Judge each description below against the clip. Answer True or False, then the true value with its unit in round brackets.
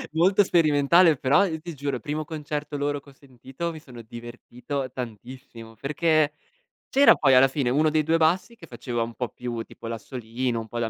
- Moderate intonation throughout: True (4.4 semitones)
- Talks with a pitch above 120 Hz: True (140 Hz)